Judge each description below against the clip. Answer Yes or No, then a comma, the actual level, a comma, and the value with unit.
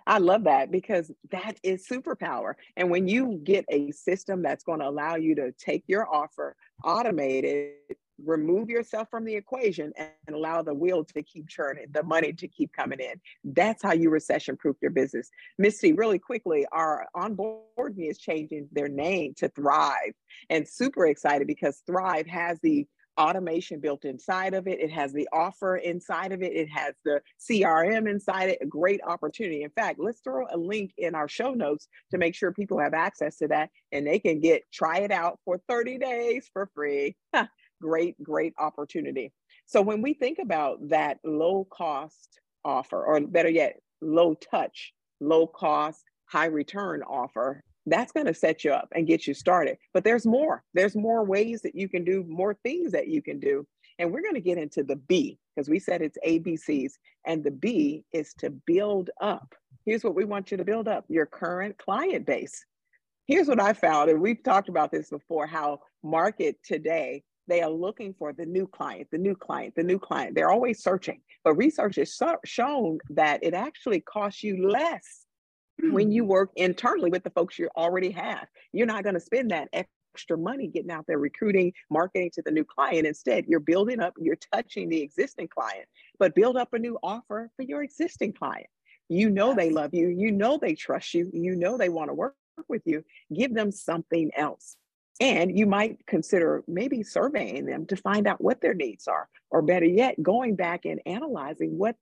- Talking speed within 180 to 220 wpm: Yes, average, 190 wpm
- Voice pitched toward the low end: No, medium, 180 Hz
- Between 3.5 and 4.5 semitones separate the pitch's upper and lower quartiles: No, average, 5.2 semitones